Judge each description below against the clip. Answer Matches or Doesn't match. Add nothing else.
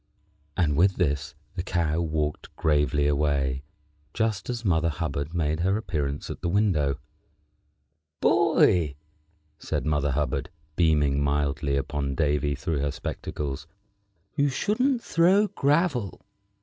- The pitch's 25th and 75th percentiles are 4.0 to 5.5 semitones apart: Matches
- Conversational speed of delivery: Doesn't match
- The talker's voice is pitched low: Matches